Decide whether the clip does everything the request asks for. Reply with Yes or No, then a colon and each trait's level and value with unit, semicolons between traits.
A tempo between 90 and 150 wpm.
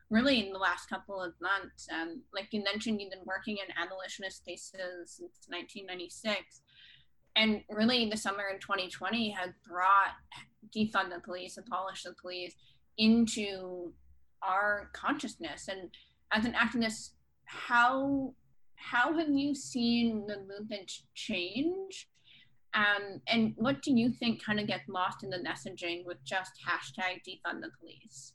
Yes: average, 140 wpm